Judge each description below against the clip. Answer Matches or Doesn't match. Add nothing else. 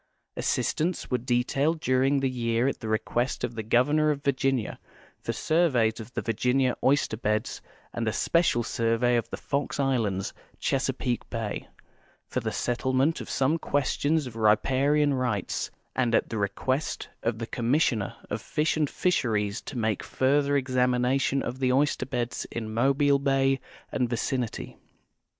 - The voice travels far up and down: Doesn't match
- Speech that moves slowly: Doesn't match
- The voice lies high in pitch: Doesn't match